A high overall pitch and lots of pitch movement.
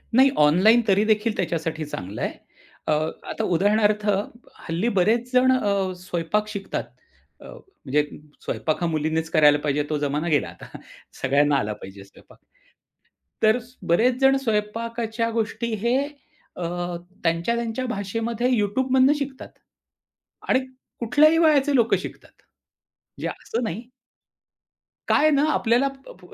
Yes: high, 215 Hz; wide, 6.6 semitones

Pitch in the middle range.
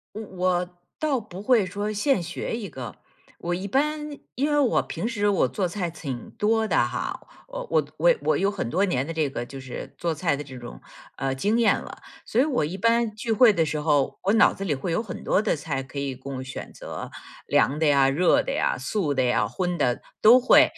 Yes: medium, 180 Hz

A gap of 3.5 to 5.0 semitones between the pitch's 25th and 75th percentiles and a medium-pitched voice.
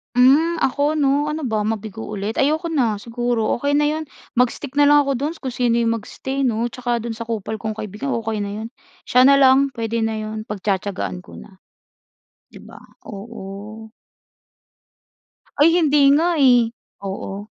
No: average, 4.4 semitones; high, 235 Hz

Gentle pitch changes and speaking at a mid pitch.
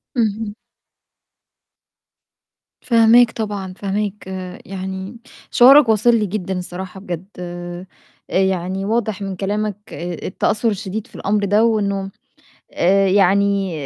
No: narrow, 2.2 semitones; high, 200 Hz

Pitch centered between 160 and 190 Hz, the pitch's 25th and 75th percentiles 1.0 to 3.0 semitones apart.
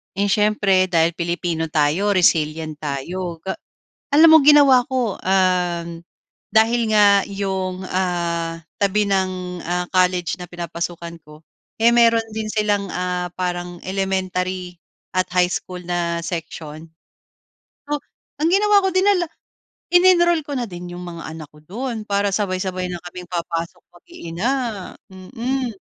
No: medium, 185 Hz; average, 3.6 semitones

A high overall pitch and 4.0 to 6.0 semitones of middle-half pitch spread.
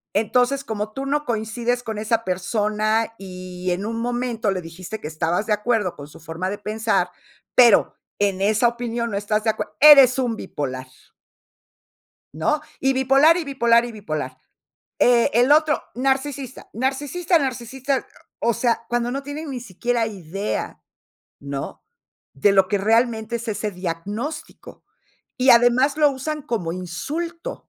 Yes: high, 230 Hz; average, 4.7 semitones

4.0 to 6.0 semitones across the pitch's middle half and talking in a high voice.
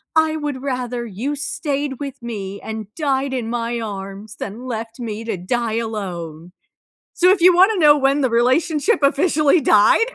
Yes: average, 5.1 semitones; very high, 250 Hz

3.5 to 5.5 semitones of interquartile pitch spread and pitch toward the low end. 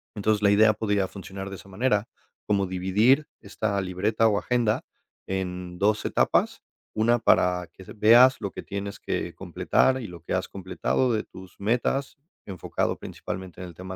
No: average, 2.8 semitones; low, 100 Hz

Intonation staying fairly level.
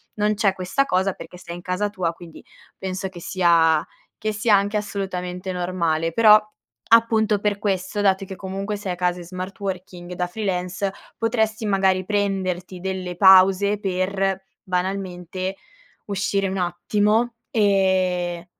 Yes: narrow, 2.1 semitones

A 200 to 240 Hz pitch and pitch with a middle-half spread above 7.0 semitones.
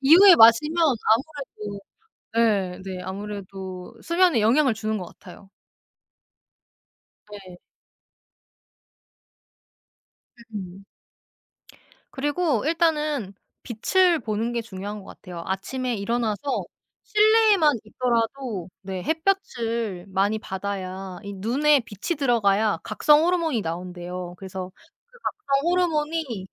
Yes: high, 225 Hz; wide, 7.5 semitones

